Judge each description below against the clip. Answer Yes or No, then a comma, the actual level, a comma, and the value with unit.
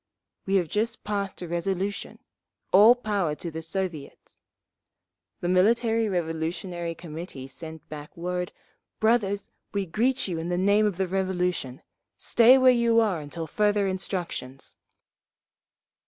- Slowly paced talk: Yes, slow, 130 wpm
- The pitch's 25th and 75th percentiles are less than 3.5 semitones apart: No, average, 3.9 semitones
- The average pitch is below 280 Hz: Yes, medium, 185 Hz